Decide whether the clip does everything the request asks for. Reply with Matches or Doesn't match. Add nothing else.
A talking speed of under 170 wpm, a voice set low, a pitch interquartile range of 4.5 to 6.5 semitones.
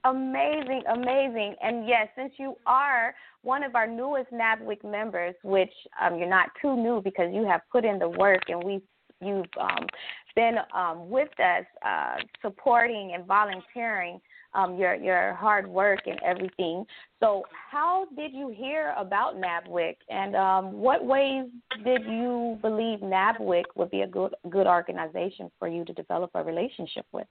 Doesn't match